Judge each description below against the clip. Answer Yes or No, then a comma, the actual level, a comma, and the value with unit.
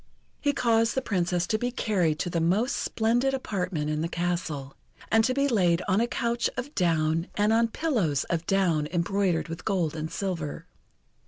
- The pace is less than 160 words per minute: No, average, 180 wpm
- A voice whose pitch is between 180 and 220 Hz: Yes, medium, 185 Hz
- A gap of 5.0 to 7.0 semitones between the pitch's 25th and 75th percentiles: Yes, wide, 5.5 semitones